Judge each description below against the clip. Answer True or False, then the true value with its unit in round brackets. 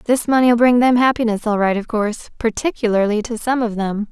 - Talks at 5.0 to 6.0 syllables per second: True (5.5 syllables/s)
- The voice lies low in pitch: False (225 Hz)